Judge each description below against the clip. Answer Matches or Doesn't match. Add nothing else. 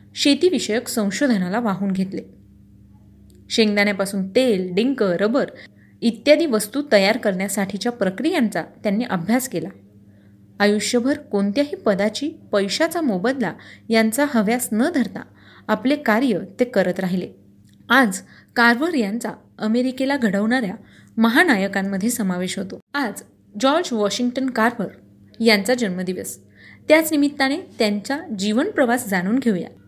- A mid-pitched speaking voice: Doesn't match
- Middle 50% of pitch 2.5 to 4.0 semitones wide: Doesn't match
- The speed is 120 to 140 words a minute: Doesn't match